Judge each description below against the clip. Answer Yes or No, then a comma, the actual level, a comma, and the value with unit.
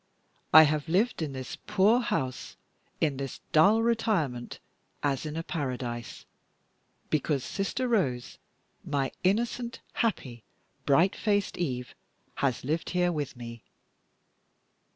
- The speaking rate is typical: No, slow, 115 wpm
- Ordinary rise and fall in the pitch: No, wide, 7.3 semitones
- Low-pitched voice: No, medium, 155 Hz